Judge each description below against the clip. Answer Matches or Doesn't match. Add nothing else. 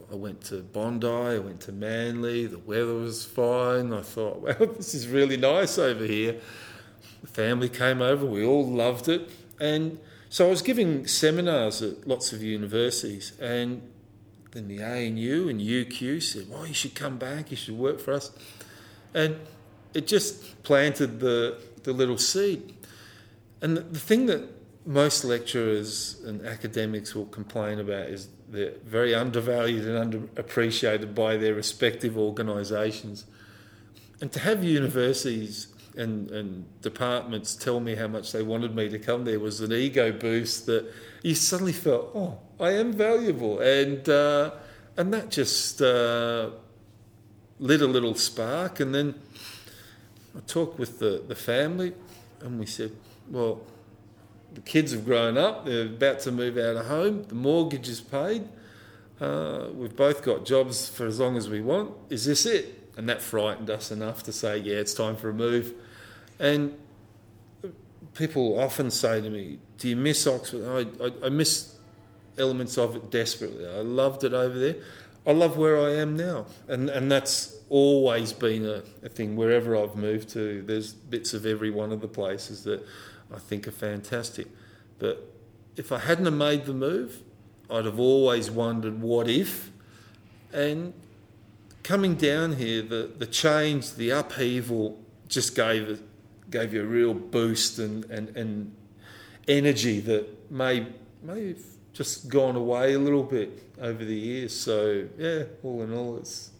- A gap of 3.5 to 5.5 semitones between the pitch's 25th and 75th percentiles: Matches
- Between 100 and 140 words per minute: Doesn't match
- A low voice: Matches